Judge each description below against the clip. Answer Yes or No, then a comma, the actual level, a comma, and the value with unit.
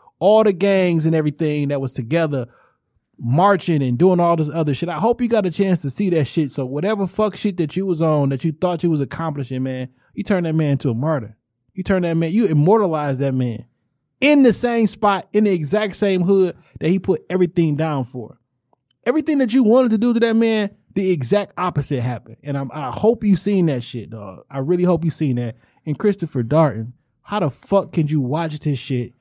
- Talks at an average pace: No, fast, 225 wpm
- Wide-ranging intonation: Yes, wide, 6.3 semitones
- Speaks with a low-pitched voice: No, medium, 165 Hz